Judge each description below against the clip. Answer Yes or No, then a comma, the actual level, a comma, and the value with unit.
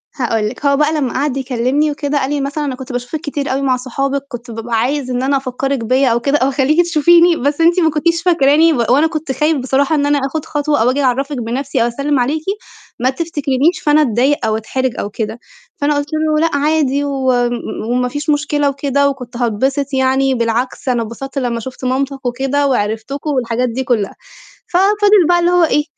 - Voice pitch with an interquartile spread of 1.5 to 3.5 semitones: Yes, average, 2.9 semitones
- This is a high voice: Yes, very high, 275 Hz